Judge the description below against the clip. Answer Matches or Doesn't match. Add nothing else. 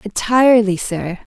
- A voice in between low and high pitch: Doesn't match